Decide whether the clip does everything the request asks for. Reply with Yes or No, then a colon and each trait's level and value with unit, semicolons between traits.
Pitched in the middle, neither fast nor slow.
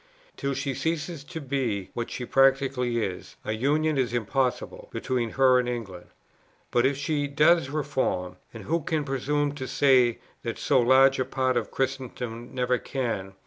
No: low, 130 Hz; average, 165 wpm